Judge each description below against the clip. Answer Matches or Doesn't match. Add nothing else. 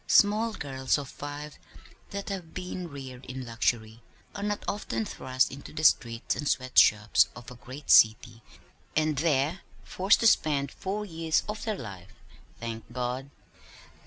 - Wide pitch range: Matches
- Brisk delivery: Doesn't match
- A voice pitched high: Doesn't match